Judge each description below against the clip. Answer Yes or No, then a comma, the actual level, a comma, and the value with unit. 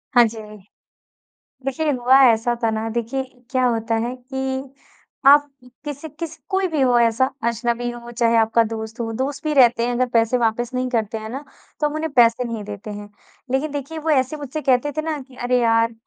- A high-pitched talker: Yes, high, 245 Hz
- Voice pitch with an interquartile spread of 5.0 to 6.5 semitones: No, average, 3.2 semitones